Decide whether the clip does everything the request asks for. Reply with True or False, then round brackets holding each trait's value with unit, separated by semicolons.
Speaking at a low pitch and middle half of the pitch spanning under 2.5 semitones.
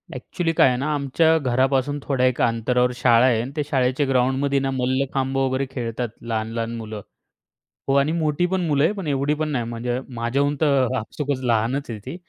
False (130 Hz; 2.8 semitones)